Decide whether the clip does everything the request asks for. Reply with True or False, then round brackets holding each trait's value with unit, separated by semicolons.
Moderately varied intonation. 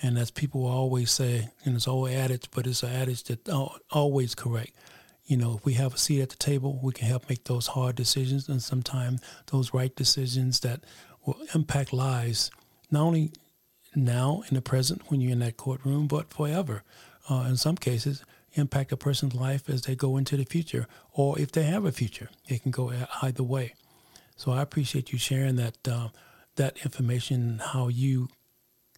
False (2.0 semitones)